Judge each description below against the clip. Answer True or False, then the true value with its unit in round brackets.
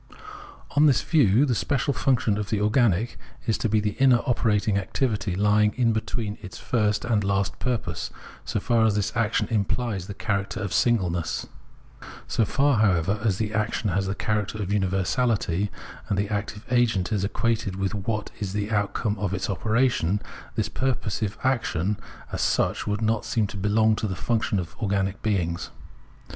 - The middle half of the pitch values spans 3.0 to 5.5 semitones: False (2.6 semitones)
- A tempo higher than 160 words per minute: True (170 wpm)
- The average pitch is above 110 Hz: False (105 Hz)